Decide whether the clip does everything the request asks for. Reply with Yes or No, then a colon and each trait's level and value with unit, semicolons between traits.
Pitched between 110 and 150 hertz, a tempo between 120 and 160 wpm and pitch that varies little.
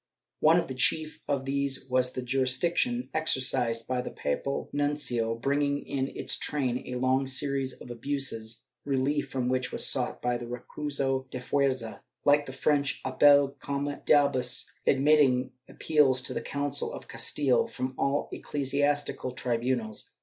Yes: low, 135 Hz; average, 150 wpm; narrow, 2.2 semitones